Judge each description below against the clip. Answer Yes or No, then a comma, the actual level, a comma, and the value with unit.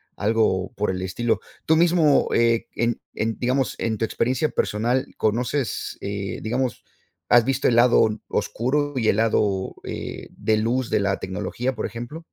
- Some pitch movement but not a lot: Yes, average, 3.1 semitones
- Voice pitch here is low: Yes, low, 115 Hz